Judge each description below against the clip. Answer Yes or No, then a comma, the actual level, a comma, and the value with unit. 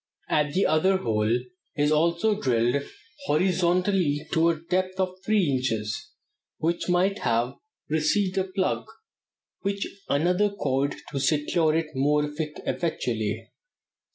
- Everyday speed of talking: No, slow, 125 wpm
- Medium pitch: Yes, medium, 155 Hz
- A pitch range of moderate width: Yes, average, 4.9 semitones